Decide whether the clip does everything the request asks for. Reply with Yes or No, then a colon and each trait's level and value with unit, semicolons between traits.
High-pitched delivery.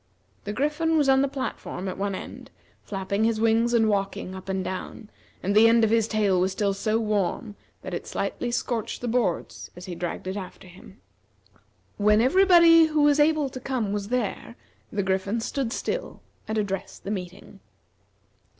Yes: high, 215 Hz